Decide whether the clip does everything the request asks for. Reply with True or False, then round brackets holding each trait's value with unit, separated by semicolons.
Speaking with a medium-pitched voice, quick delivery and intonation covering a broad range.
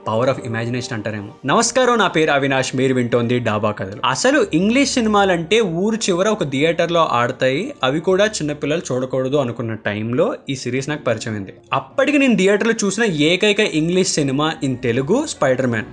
True (150 Hz; 175 wpm; 7.8 semitones)